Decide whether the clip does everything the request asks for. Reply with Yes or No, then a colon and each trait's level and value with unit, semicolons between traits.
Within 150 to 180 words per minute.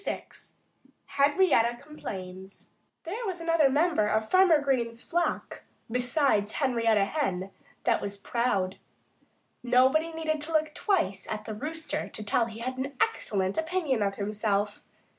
No: average, 140 wpm